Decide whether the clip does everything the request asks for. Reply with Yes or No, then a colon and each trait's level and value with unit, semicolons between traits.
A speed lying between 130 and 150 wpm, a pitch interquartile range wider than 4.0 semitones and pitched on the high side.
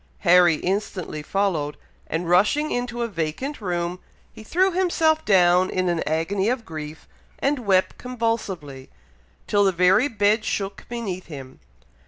Yes: average, 140 wpm; average, 5.2 semitones; high, 195 Hz